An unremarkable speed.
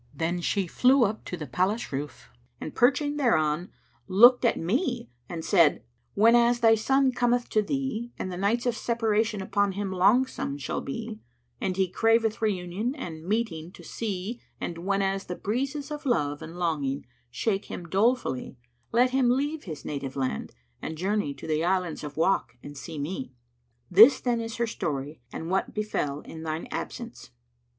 Yes: average, 170 wpm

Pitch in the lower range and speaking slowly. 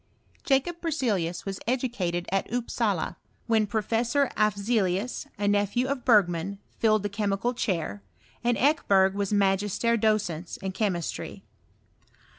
No: high, 205 Hz; slow, 115 wpm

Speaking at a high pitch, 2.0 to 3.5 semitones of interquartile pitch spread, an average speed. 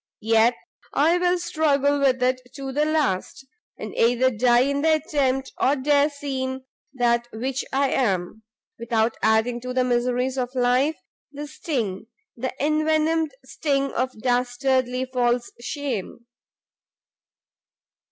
No: very high, 260 Hz; average, 2.8 semitones; slow, 125 wpm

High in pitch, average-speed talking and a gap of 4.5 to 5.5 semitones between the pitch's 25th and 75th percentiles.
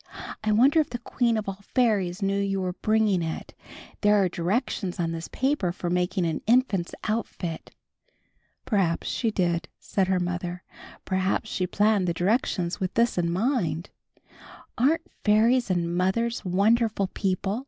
No: high, 195 Hz; average, 155 wpm; average, 4.0 semitones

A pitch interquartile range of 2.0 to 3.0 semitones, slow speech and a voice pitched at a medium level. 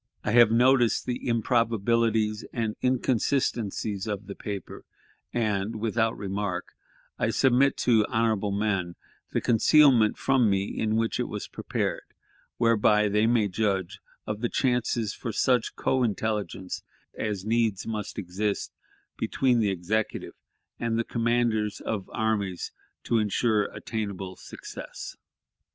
No: narrow, 2.4 semitones; slow, 125 wpm; low, 110 Hz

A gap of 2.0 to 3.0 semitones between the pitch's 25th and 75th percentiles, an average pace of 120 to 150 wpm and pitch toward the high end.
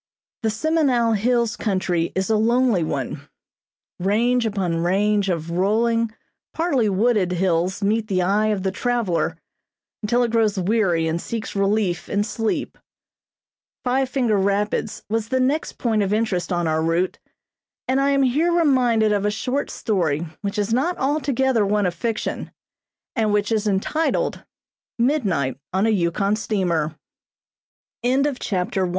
No: average, 4.1 semitones; average, 140 wpm; high, 210 Hz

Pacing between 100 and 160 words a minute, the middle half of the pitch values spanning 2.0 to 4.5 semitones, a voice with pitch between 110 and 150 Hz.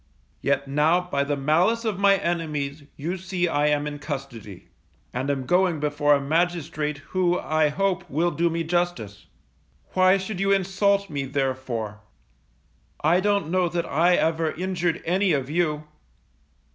No: average, 155 wpm; average, 4.1 semitones; medium, 160 Hz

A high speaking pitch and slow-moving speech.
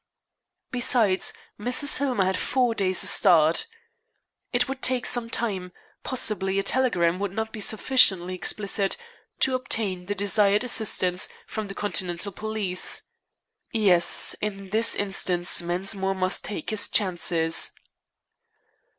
Yes: high, 200 Hz; slow, 120 wpm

